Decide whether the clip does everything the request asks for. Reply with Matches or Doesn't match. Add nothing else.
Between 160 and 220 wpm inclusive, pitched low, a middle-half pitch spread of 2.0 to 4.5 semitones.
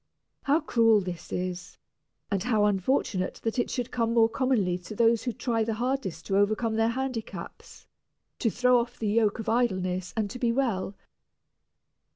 Doesn't match